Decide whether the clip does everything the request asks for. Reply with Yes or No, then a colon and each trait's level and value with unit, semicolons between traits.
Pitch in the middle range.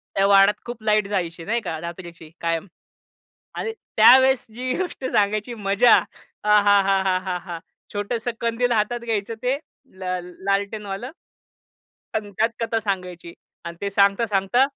No: high, 205 Hz